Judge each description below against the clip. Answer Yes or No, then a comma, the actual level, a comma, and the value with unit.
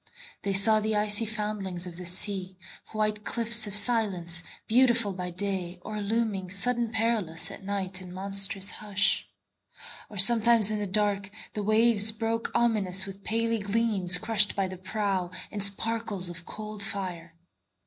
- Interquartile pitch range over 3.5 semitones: No, narrow, 2.6 semitones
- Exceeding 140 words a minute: No, slow, 135 wpm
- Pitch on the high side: Yes, high, 205 Hz